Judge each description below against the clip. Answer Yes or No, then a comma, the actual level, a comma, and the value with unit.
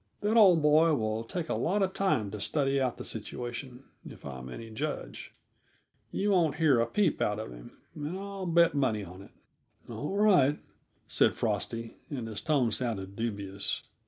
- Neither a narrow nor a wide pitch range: No, wide, 7.4 semitones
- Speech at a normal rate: Yes, average, 175 wpm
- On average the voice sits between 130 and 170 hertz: Yes, low, 135 Hz